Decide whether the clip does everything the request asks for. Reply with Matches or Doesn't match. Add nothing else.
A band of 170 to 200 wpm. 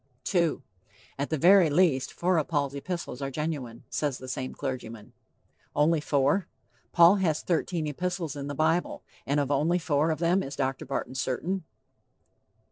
Doesn't match